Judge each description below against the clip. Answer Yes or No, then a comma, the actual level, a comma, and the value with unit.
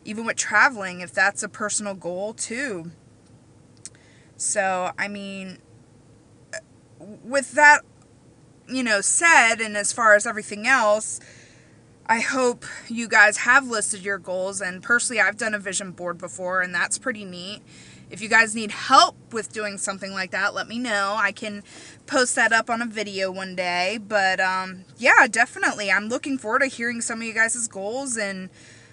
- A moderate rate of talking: Yes, average, 170 wpm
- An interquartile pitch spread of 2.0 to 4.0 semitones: Yes, average, 3.4 semitones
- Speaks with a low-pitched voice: No, high, 205 Hz